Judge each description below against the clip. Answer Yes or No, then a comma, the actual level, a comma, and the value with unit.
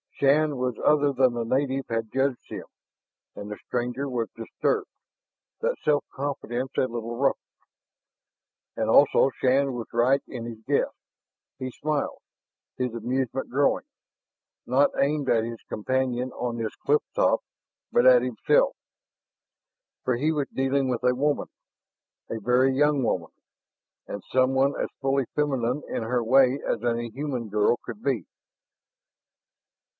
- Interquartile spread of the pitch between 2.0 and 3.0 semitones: Yes, average, 2.7 semitones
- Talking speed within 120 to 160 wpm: Yes, average, 140 wpm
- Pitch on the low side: Yes, low, 130 Hz